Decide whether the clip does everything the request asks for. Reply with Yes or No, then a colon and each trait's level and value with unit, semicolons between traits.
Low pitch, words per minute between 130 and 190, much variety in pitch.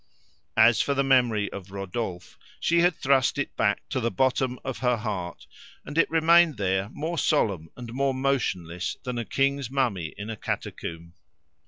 Yes: low, 125 Hz; average, 170 wpm; wide, 5.7 semitones